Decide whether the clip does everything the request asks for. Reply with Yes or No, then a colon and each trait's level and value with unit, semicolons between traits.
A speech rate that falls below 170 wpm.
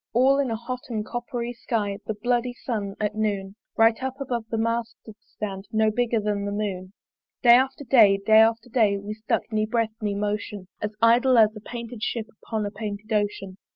No: average, 200 wpm